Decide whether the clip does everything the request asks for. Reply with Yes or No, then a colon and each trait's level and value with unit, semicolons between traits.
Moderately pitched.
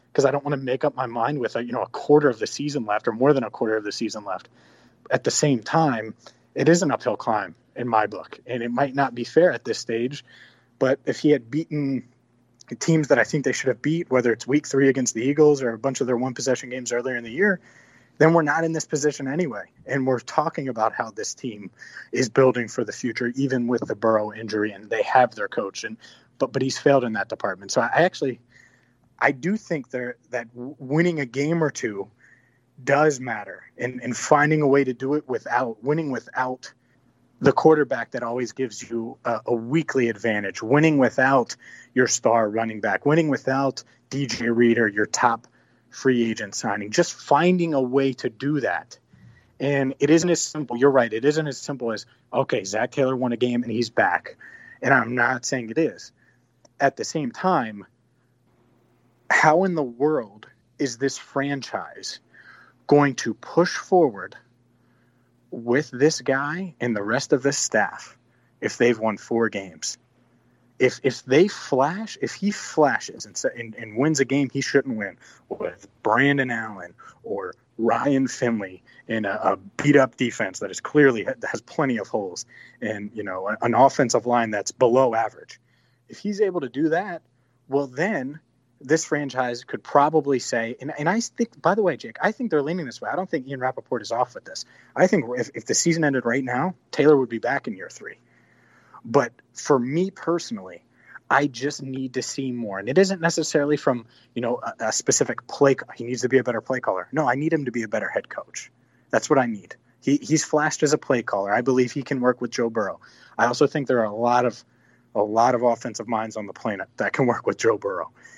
No: low, 130 Hz